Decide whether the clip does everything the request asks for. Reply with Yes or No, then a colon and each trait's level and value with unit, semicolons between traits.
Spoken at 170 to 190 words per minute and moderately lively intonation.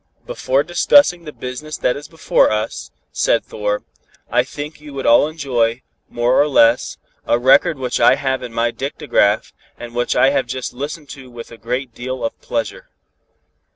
Yes: average, 175 wpm; average, 3.7 semitones